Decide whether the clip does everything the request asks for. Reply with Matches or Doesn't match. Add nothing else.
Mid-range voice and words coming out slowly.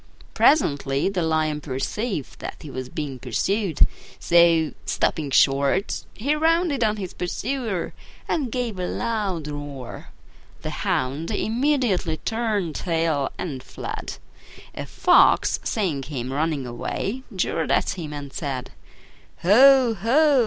Matches